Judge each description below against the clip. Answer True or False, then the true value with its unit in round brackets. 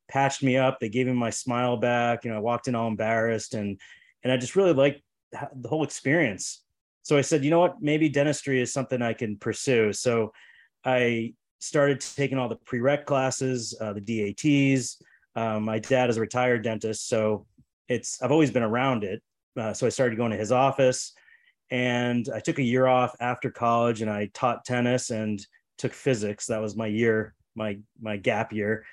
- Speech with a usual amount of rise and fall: True (3.0 semitones)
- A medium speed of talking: True (195 wpm)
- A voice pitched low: True (120 Hz)